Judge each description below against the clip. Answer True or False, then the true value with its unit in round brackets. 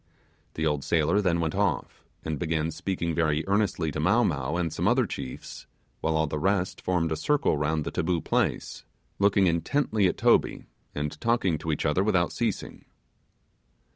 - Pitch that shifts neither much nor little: True (3.7 semitones)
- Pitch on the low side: True (85 Hz)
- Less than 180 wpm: True (170 wpm)